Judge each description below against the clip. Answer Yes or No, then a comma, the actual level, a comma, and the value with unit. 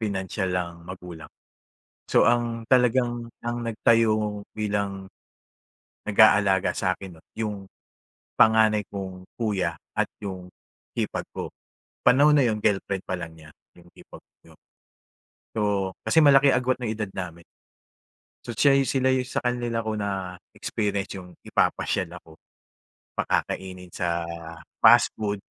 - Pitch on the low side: Yes, low, 105 Hz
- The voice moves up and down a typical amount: Yes, average, 4.0 semitones